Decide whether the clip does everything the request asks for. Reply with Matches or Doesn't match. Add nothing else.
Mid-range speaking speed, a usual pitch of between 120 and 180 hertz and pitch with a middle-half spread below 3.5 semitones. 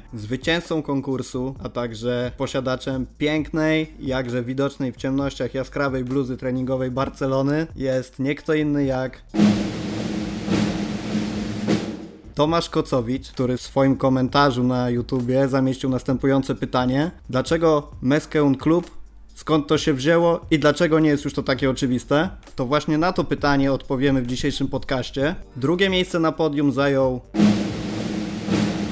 Matches